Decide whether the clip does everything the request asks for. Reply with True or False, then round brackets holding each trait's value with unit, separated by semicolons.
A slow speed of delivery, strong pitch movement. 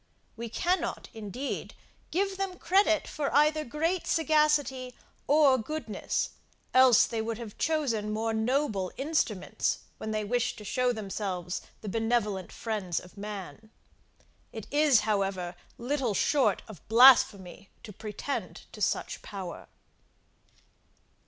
True (120 wpm; 5.8 semitones)